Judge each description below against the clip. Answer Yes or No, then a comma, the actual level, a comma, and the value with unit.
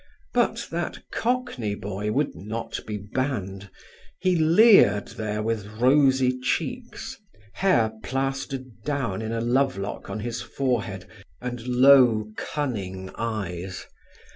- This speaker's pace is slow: Yes, slow, 115 wpm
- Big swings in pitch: No, average, 4.5 semitones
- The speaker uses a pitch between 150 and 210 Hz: No, low, 120 Hz